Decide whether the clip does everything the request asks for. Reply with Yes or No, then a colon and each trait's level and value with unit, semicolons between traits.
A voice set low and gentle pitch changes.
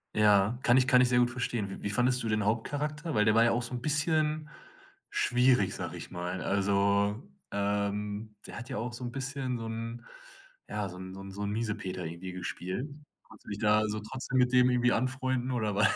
No: low, 115 Hz; average, 3.8 semitones